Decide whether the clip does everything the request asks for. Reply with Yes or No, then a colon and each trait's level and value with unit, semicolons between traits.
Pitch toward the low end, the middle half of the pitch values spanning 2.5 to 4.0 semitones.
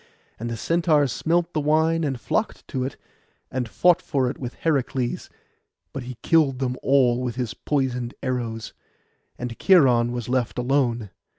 Yes: low, 130 Hz; average, 3.7 semitones